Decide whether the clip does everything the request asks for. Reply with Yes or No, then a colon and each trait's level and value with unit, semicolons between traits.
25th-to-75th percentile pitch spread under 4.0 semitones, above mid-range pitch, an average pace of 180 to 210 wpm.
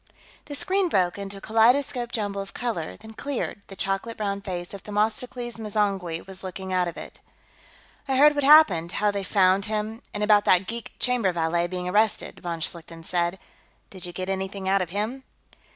Yes: average, 3.4 semitones; high, 200 Hz; average, 185 wpm